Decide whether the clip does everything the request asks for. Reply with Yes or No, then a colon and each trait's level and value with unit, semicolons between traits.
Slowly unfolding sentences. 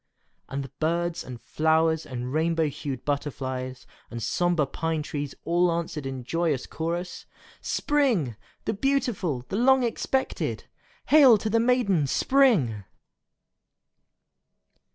Yes: slow, 110 wpm